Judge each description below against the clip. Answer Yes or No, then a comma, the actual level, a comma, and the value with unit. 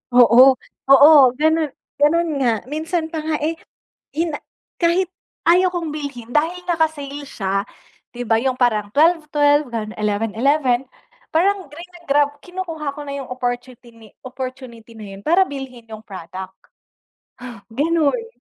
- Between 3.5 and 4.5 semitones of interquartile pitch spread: No, average, 5.1 semitones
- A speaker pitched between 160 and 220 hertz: No, very high, 285 Hz